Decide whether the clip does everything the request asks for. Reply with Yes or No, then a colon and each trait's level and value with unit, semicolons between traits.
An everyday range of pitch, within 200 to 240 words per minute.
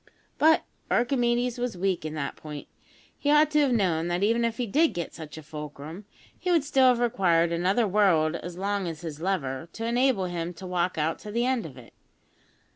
No: wide, 6.5 semitones; fast, 205 wpm